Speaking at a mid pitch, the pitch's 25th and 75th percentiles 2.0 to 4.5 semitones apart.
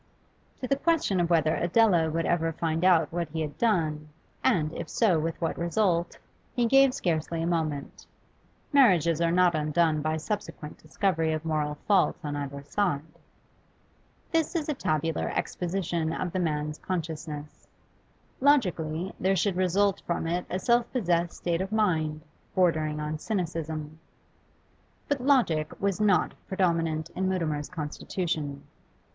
Yes: medium, 170 Hz; average, 3.4 semitones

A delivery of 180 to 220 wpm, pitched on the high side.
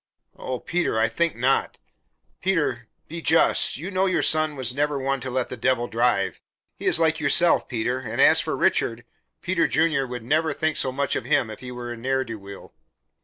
No: fast, 205 wpm; low, 130 Hz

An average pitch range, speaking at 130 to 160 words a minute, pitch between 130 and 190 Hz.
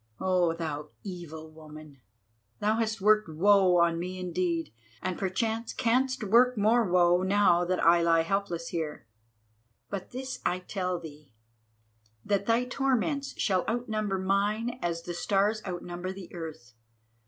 Yes: average, 4.1 semitones; average, 140 wpm; medium, 185 Hz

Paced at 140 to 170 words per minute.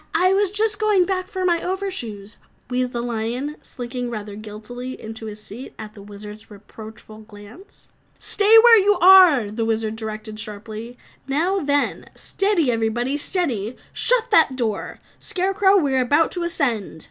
Yes: average, 160 wpm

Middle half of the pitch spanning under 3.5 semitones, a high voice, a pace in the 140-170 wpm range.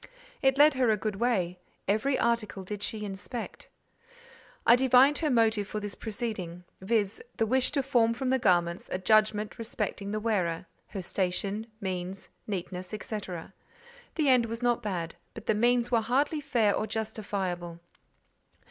No: average, 3.9 semitones; high, 215 Hz; average, 155 wpm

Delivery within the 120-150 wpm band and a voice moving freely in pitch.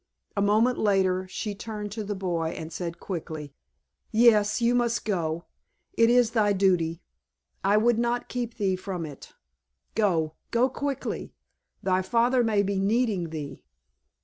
No: average, 140 wpm; average, 4.4 semitones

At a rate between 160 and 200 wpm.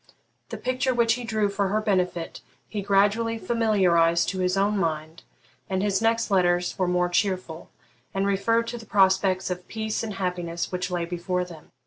Yes: average, 175 wpm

